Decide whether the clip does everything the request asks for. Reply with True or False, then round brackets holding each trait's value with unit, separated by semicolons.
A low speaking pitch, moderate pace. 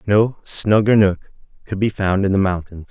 True (100 Hz; 185 wpm)